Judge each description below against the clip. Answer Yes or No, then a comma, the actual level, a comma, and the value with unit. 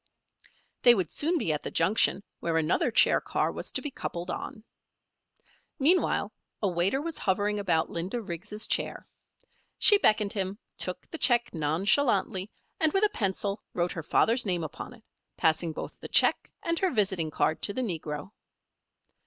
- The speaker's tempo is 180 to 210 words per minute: No, average, 165 wpm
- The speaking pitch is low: No, high, 200 Hz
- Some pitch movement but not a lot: No, wide, 6.1 semitones